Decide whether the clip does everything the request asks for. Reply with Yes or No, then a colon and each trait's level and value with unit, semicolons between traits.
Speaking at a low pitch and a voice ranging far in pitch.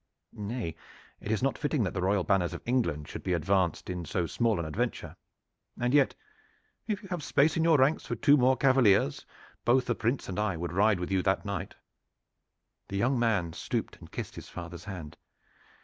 Yes: low, 105 Hz; wide, 6.4 semitones